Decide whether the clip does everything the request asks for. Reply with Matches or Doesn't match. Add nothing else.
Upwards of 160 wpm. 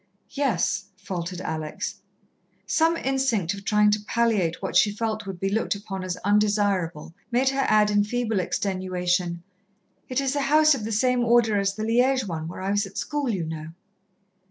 Matches